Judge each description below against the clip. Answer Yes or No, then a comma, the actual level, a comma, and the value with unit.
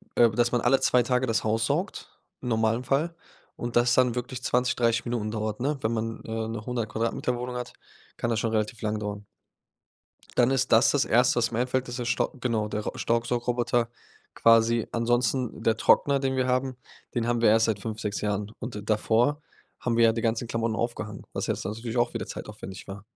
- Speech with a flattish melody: Yes, narrow, 1.9 semitones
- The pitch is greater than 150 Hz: No, low, 115 Hz